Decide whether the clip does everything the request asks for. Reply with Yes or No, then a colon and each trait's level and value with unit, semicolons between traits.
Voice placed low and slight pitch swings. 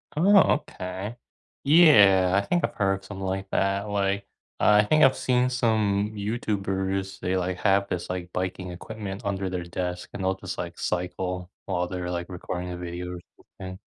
Yes: very low, 95 Hz; narrow, 2.3 semitones